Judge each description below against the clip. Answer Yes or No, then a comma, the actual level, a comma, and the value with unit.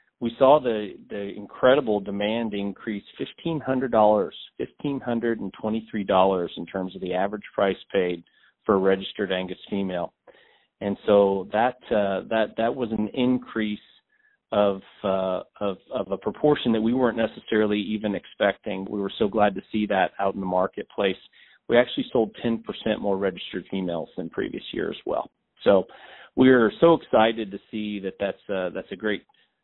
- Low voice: Yes, low, 105 Hz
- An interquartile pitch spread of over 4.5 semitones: No, average, 2.9 semitones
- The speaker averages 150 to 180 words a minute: Yes, average, 175 wpm